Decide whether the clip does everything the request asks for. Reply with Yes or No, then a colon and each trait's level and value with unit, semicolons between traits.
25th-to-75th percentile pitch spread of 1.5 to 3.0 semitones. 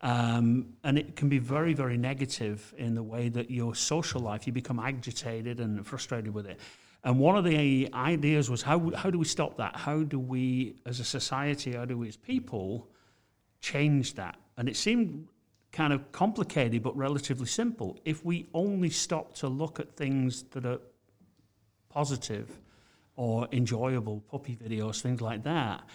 No: average, 4.1 semitones